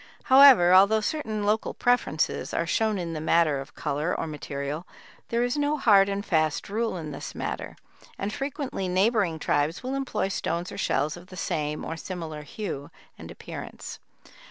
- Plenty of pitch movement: Yes, wide, 5.9 semitones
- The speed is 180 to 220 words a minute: No, average, 170 wpm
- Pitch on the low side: No, medium, 185 Hz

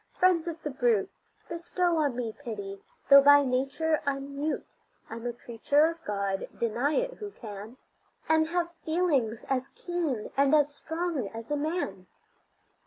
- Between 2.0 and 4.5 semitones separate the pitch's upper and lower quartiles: No, wide, 5.5 semitones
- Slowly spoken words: No, average, 155 wpm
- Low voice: No, very high, 280 Hz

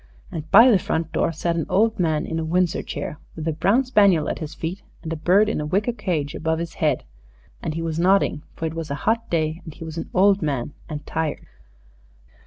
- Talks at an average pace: No, fast, 230 wpm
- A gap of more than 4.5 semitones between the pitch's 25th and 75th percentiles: No, average, 3.5 semitones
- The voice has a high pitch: No, medium, 165 Hz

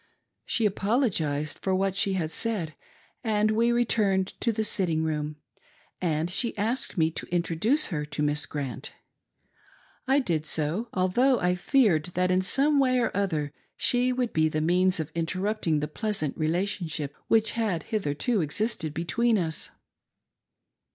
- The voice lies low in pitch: No, medium, 185 Hz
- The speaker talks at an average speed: Yes, average, 150 wpm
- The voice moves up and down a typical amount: No, wide, 5.9 semitones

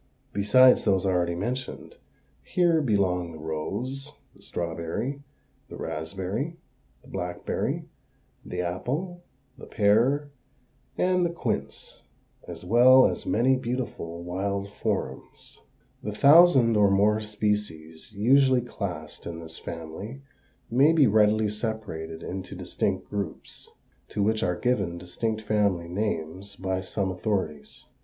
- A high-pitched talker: No, low, 105 Hz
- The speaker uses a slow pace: Yes, slow, 120 wpm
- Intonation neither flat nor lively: No, wide, 5.8 semitones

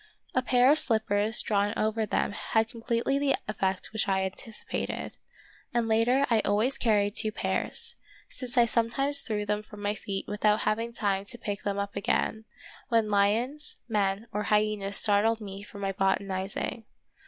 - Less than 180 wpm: Yes, average, 165 wpm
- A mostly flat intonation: Yes, narrow, 2.3 semitones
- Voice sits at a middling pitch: No, high, 215 Hz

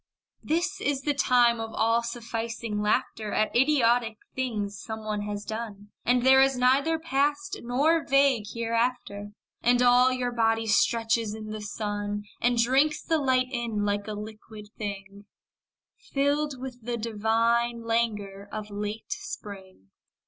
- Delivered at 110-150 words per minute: Yes, average, 140 wpm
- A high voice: Yes, high, 230 Hz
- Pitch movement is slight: No, average, 3.3 semitones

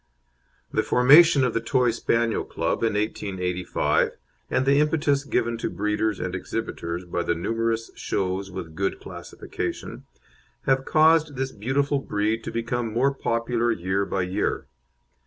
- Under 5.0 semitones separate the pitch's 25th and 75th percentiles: No, average, 5.3 semitones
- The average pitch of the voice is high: No, low, 115 Hz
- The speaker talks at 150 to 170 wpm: No, average, 140 wpm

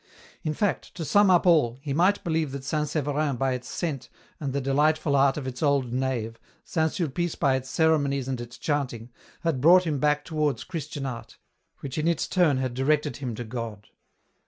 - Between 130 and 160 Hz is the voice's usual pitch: Yes, medium, 140 Hz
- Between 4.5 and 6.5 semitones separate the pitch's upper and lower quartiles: No, average, 3.4 semitones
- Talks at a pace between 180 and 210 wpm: Yes, average, 195 wpm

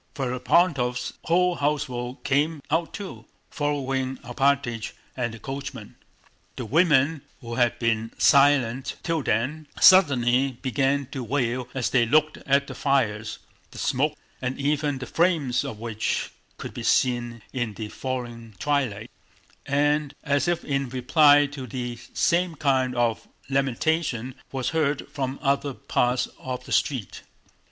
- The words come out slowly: Yes, slow, 130 wpm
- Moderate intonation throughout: Yes, average, 3.1 semitones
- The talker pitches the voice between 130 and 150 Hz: Yes, low, 135 Hz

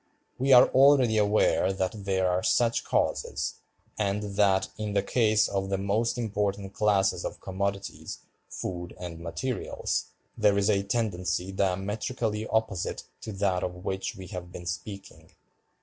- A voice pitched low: Yes, low, 100 Hz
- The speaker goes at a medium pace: Yes, average, 145 wpm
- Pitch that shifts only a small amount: Yes, narrow, 2.3 semitones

